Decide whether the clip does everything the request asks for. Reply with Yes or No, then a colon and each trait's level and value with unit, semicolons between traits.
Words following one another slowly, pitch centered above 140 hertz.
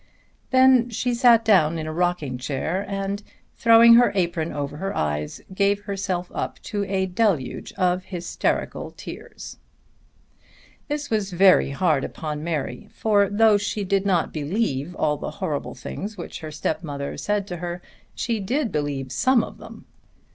No: average, 155 wpm; medium, 185 Hz